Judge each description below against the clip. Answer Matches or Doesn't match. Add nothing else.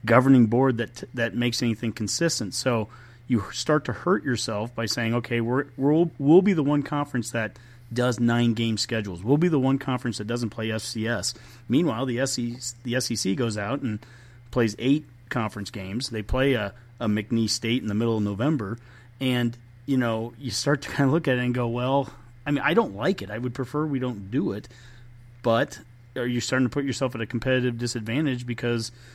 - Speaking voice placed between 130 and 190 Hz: Doesn't match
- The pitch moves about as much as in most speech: Doesn't match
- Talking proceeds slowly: Doesn't match